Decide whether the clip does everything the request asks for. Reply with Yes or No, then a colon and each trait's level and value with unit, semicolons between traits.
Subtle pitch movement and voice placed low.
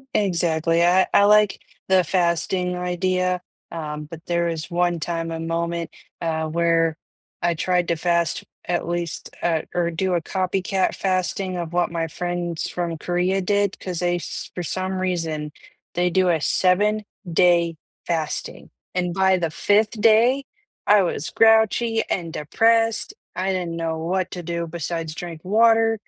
No: narrow, 2.2 semitones; medium, 175 Hz